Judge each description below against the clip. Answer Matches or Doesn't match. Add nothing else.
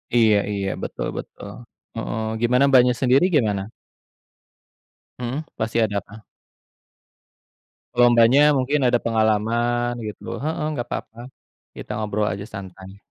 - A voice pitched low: Matches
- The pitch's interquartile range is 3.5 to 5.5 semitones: Doesn't match